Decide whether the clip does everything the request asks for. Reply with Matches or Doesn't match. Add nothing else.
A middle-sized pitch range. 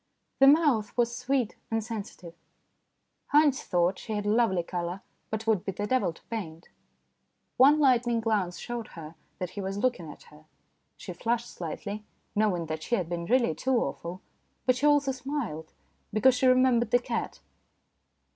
Doesn't match